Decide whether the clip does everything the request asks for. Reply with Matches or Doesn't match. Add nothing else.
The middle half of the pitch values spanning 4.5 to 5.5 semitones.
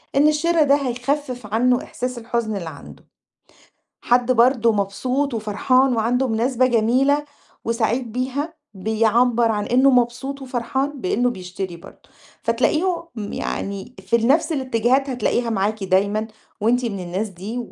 Doesn't match